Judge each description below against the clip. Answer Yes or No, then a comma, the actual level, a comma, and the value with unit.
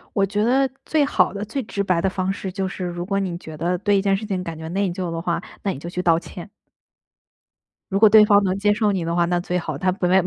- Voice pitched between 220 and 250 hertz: No, high, 190 Hz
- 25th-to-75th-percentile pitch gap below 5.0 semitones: Yes, narrow, 2.6 semitones